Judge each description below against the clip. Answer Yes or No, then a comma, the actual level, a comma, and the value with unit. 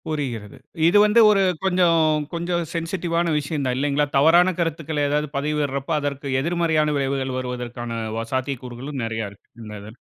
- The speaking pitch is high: No, medium, 145 Hz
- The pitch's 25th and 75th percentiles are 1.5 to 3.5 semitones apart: No, average, 4.3 semitones